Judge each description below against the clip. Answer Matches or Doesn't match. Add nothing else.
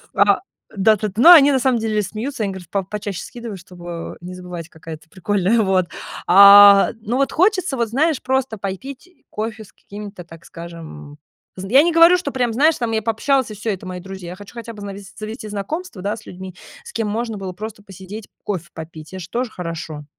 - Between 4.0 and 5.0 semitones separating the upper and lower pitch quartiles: Matches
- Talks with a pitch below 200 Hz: Doesn't match